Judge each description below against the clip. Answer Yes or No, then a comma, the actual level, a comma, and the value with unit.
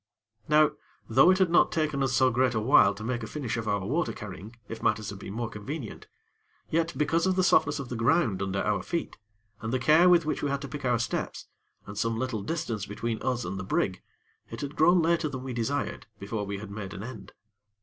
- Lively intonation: Yes, wide, 5.9 semitones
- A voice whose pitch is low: Yes, low, 120 Hz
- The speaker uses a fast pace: Yes, fast, 230 wpm